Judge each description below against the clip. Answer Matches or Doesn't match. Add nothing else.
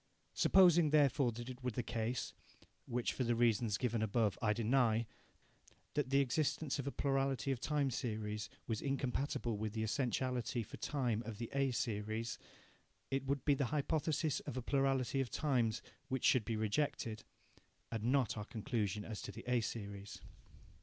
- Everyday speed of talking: Matches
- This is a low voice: Matches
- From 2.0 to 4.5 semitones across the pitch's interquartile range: Matches